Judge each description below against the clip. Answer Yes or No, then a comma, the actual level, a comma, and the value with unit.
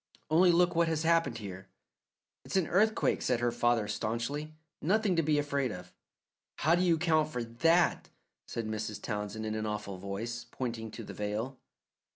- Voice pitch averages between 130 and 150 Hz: No, low, 120 Hz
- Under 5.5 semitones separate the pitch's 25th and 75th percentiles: No, wide, 7.1 semitones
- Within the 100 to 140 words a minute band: No, average, 175 wpm